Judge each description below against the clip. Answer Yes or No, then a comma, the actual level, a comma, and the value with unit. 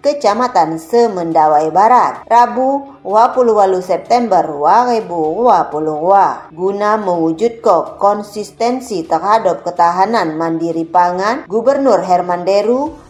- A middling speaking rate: No, slow, 80 wpm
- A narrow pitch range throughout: No, wide, 5.5 semitones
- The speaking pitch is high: Yes, high, 200 Hz